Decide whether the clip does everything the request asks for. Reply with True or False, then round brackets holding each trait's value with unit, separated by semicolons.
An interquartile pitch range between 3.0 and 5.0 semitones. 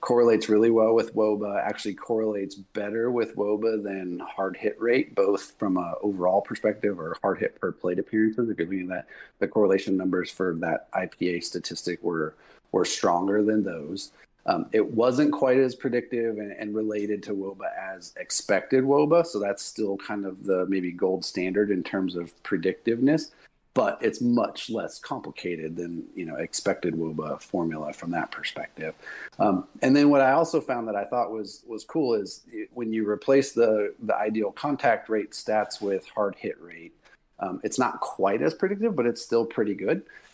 True (3.7 semitones)